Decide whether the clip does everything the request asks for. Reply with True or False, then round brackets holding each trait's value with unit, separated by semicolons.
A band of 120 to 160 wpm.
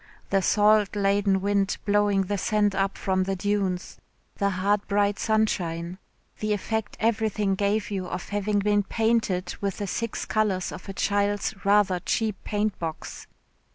True (155 wpm)